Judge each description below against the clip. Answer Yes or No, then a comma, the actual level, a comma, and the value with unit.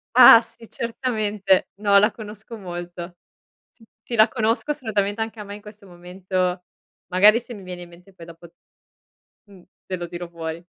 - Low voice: No, high, 200 Hz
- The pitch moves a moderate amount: Yes, average, 3.7 semitones